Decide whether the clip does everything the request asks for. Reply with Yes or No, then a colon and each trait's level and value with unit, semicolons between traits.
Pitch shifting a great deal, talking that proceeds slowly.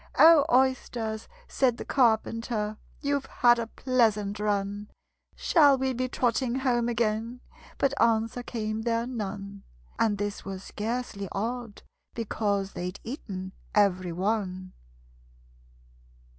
No: average, 3.3 semitones; slow, 115 wpm